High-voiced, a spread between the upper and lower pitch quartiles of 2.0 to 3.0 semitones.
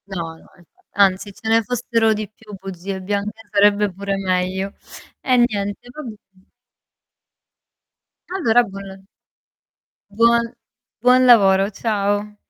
Yes: high, 205 Hz; average, 2.7 semitones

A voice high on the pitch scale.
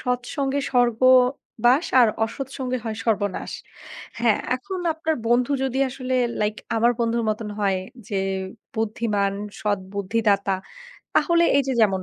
Yes: high, 235 Hz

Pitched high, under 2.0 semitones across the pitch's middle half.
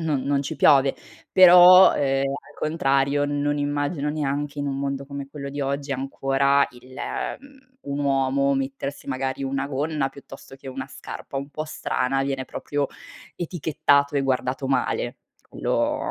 No: medium, 140 Hz; narrow, 1.2 semitones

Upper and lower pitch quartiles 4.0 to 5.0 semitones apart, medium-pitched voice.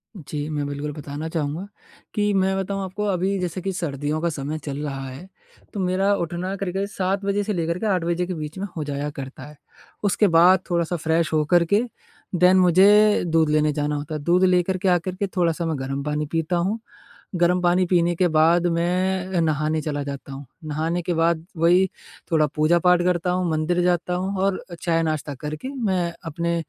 No: average, 3.2 semitones; medium, 170 Hz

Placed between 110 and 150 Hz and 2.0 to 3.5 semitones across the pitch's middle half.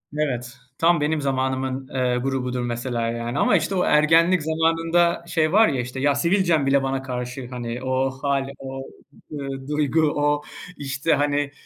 Yes: low, 135 Hz; average, 3.2 semitones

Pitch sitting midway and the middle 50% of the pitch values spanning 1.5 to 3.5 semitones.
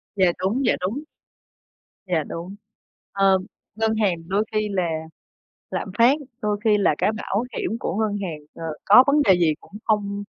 No: high, 205 Hz; narrow, 2.4 semitones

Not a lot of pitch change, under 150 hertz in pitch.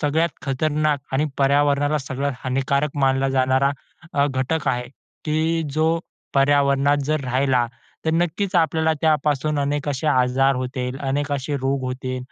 Yes: narrow, 2.3 semitones; medium, 140 Hz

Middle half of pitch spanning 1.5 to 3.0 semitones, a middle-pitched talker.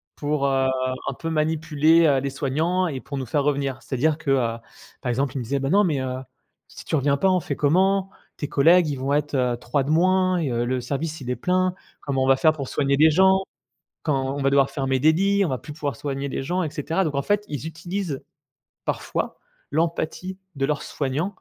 No: average, 3.5 semitones; medium, 145 Hz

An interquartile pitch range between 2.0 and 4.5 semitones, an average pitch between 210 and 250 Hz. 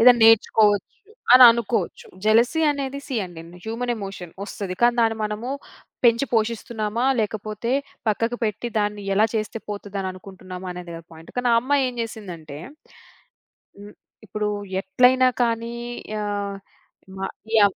Yes: average, 2.9 semitones; high, 215 Hz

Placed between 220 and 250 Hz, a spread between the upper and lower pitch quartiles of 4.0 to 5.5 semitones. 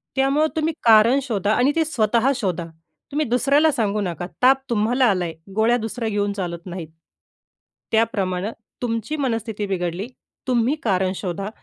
Yes: high, 225 Hz; average, 4.6 semitones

